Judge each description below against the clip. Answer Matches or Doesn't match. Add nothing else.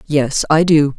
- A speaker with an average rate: Matches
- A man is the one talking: Doesn't match